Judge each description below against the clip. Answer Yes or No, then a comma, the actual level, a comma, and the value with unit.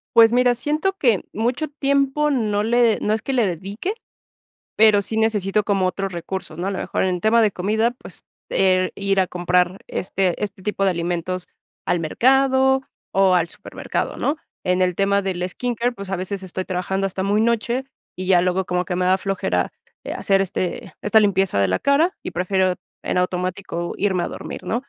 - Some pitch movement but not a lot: Yes, average, 3.9 semitones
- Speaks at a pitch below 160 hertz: No, high, 195 Hz